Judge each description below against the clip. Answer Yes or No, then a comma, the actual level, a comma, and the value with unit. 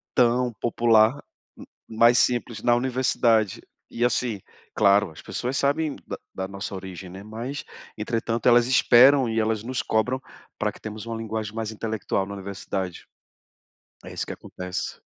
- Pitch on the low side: Yes, low, 115 Hz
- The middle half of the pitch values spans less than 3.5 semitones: Yes, average, 2.9 semitones